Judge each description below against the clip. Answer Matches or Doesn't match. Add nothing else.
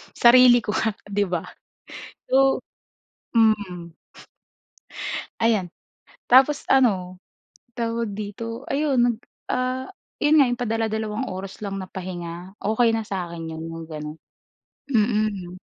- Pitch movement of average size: Matches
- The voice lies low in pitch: Doesn't match